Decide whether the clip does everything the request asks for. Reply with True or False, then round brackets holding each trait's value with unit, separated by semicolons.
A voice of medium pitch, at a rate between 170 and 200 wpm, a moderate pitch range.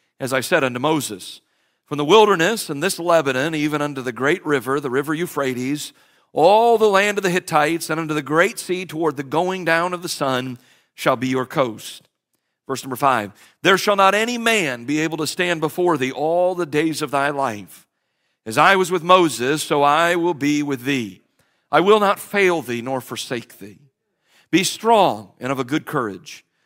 True (155 Hz; 195 wpm; 4.8 semitones)